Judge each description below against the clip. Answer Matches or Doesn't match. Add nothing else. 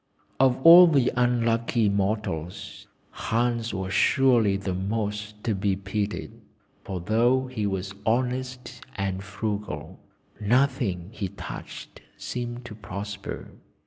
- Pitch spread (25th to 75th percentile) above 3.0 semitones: Matches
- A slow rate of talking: Matches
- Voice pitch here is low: Matches